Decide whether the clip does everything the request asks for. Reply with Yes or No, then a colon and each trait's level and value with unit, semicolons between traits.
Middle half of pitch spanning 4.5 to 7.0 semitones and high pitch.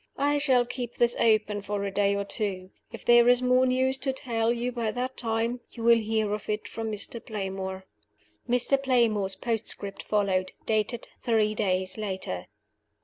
No: average, 3.2 semitones; high, 225 Hz